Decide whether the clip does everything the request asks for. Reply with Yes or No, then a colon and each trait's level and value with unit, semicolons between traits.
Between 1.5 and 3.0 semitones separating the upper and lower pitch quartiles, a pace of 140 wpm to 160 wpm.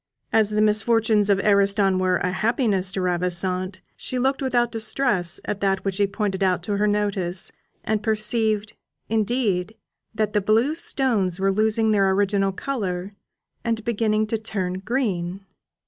Yes: narrow, 2.6 semitones; average, 150 wpm